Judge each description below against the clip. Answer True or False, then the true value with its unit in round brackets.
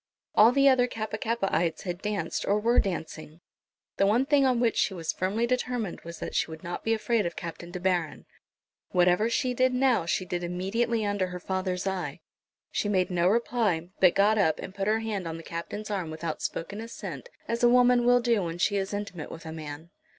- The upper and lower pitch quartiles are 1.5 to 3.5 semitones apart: False (4.9 semitones)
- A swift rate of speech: True (210 wpm)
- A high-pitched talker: True (195 Hz)